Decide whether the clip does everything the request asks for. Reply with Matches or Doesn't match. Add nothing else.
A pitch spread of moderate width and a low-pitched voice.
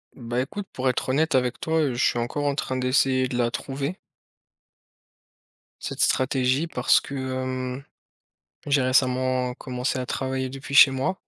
Doesn't match